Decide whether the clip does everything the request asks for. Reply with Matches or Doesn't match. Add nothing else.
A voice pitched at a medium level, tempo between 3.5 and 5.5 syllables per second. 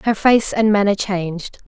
Doesn't match